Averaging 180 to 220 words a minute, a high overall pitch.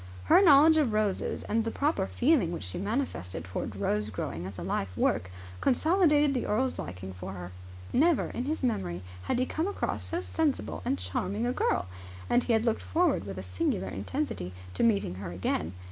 Yes: average, 190 wpm; high, 215 Hz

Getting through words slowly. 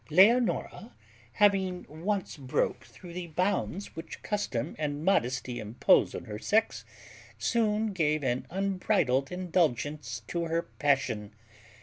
Yes: slow, 120 wpm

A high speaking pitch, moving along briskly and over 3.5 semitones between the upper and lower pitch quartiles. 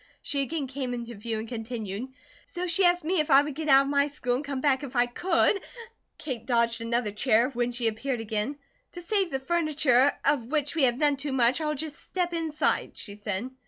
Yes: very high, 270 Hz; fast, 220 wpm; average, 4.2 semitones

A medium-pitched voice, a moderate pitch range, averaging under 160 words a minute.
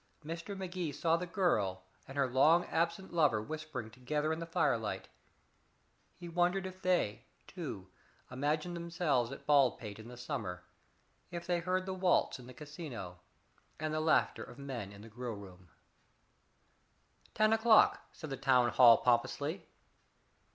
No: medium, 150 Hz; wide, 6.3 semitones; average, 150 wpm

